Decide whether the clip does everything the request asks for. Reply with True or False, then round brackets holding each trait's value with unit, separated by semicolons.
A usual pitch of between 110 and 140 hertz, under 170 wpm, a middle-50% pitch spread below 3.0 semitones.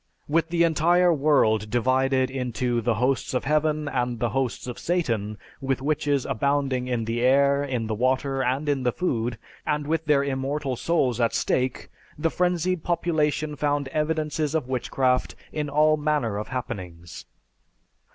False (135 Hz; 155 wpm; 3.5 semitones)